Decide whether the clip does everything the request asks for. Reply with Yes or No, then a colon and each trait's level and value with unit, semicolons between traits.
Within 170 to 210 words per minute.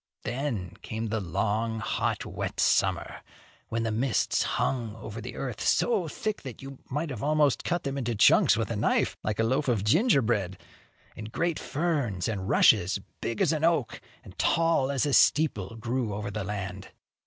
Yes: average, 175 wpm